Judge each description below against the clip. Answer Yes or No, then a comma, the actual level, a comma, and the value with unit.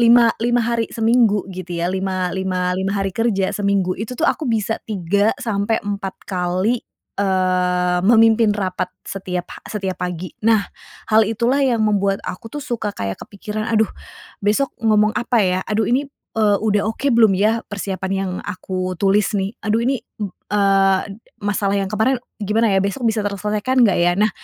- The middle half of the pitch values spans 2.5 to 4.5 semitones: Yes, average, 2.9 semitones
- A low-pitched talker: No, high, 205 Hz